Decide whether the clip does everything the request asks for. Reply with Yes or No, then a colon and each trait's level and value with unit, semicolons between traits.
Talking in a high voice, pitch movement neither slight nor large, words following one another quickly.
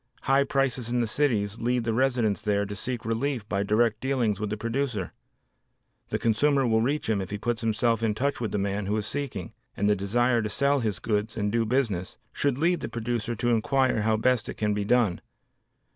No: low, 115 Hz; average, 3.4 semitones; fast, 215 wpm